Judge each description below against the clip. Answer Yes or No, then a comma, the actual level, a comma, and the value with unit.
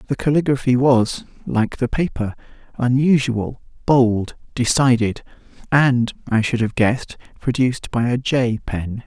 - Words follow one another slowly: Yes, slow, 125 wpm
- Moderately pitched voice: No, low, 125 Hz